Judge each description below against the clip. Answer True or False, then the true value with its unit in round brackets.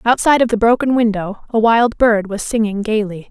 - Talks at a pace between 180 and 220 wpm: True (200 wpm)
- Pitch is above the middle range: True (220 Hz)